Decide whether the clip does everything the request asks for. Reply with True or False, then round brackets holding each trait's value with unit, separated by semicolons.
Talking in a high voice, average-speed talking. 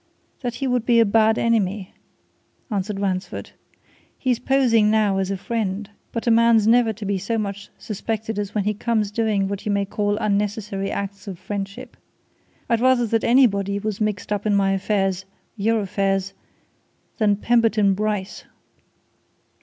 True (210 Hz; 160 wpm)